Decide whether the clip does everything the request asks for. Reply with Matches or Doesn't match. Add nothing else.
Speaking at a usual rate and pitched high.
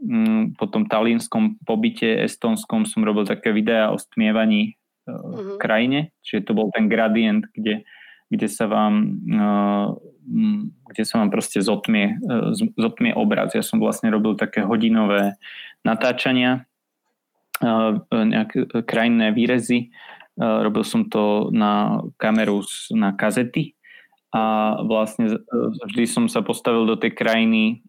Doesn't match